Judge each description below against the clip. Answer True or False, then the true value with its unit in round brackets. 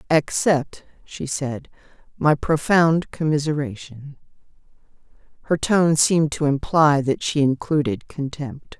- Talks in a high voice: False (145 Hz)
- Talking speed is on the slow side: True (100 wpm)